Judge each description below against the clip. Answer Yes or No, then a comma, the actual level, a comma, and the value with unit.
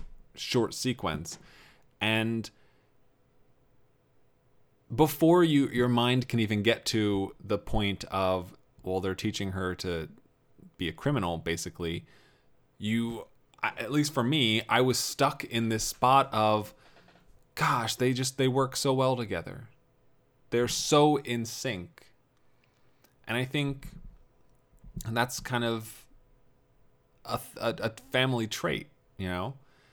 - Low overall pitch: Yes, low, 125 Hz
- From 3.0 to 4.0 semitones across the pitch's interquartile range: Yes, average, 3.4 semitones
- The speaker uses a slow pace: Yes, slow, 120 wpm